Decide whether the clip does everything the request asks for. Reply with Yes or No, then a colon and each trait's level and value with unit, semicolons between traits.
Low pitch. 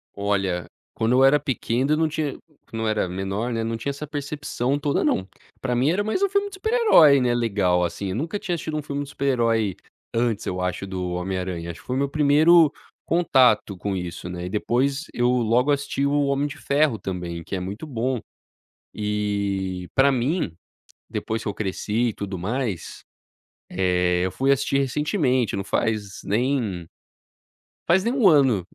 Yes: low, 120 Hz